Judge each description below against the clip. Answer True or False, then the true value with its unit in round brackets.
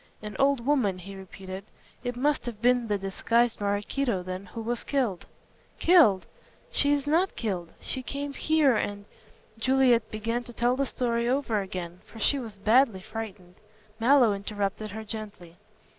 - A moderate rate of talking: True (160 wpm)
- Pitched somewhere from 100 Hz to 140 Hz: False (225 Hz)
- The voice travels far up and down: False (4.5 semitones)